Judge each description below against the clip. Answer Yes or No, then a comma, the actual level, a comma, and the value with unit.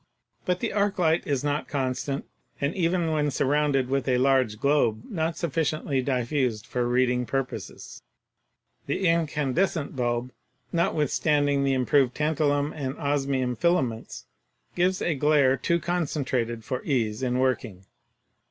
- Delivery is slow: Yes, slow, 130 wpm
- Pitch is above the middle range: No, medium, 140 Hz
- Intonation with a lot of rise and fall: No, average, 3.4 semitones